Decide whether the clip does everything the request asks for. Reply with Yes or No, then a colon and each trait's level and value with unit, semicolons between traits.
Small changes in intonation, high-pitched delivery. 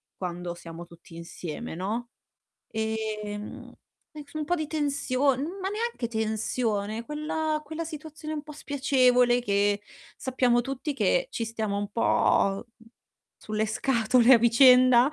No: average, 5.2 semitones; high, 240 Hz